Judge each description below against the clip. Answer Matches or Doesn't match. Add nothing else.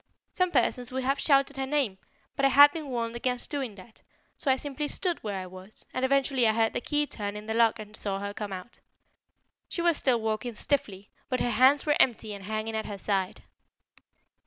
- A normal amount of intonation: Matches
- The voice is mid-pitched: Doesn't match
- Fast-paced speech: Matches